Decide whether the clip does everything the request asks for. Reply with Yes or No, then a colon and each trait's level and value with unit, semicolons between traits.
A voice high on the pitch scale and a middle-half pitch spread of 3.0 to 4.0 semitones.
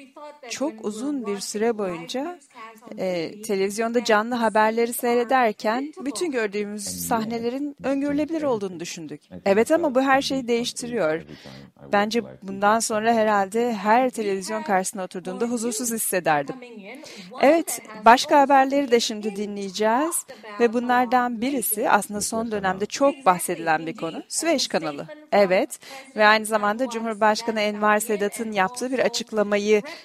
Yes: high, 225 Hz; average, 3.6 semitones